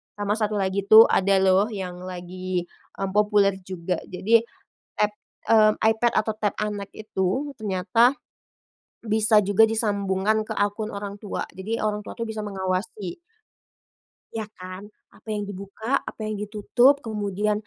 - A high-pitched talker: Yes, high, 205 Hz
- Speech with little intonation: Yes, narrow, 2.2 semitones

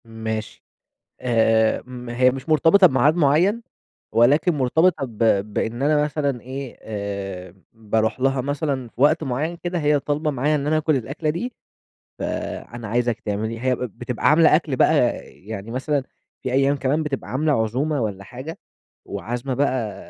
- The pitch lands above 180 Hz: No, low, 130 Hz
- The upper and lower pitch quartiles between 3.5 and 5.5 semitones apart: Yes, average, 4.7 semitones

